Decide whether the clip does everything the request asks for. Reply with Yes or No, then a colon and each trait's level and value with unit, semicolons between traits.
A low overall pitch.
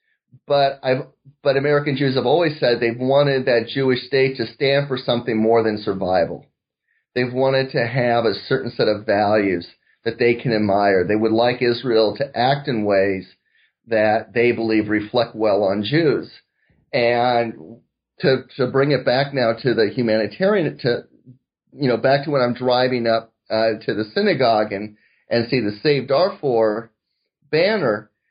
Yes: low, 120 Hz